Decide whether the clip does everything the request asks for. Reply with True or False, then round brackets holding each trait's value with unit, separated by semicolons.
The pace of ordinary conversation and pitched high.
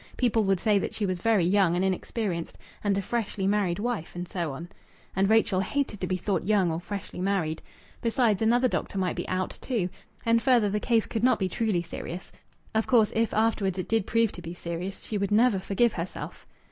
False (210 wpm; 200 Hz)